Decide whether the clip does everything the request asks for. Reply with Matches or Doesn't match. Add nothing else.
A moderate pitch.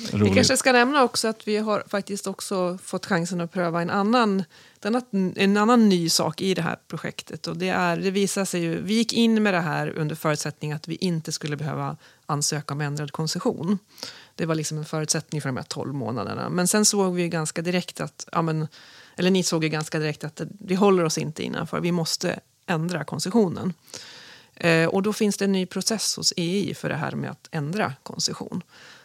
Matches